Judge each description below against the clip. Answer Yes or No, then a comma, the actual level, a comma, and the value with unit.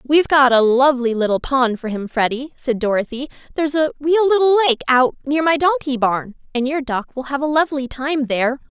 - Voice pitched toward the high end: Yes, very high, 270 Hz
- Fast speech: Yes, fast, 215 wpm